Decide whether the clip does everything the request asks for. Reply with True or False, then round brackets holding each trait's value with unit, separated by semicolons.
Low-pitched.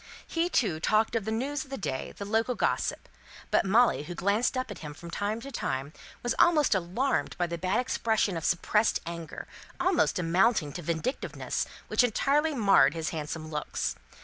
False (205 Hz)